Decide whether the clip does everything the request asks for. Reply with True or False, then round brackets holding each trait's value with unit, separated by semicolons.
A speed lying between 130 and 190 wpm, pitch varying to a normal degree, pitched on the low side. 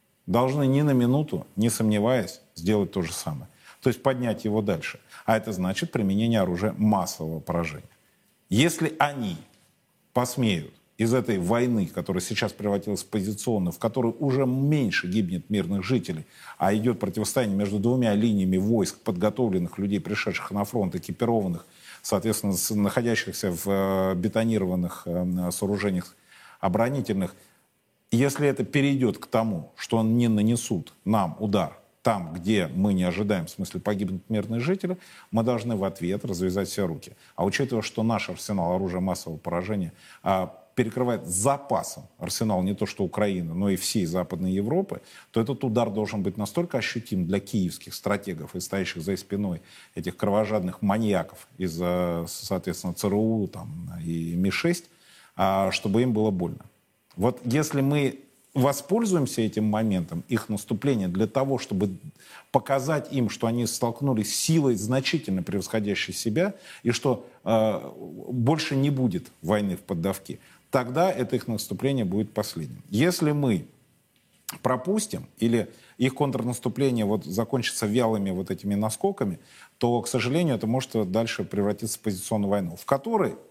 True (140 wpm; 4.4 semitones; 110 Hz)